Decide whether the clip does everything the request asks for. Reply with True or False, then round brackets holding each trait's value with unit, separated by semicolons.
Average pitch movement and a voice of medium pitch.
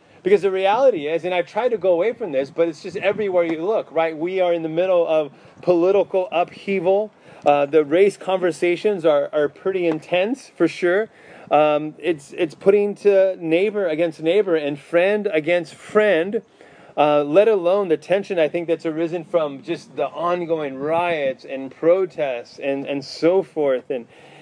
True (3.6 semitones; 175 Hz)